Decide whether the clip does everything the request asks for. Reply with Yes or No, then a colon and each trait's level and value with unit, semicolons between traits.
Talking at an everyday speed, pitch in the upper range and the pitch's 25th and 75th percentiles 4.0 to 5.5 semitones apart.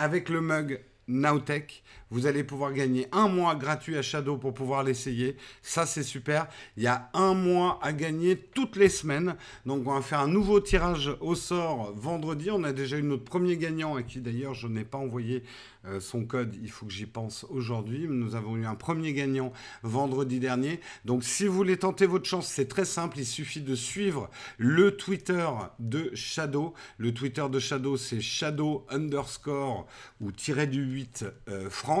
No: average, 185 wpm; medium, 140 Hz; average, 4.6 semitones